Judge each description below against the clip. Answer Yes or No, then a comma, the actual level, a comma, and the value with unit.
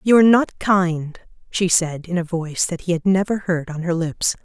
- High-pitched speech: No, medium, 175 Hz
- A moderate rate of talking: No, fast, 215 wpm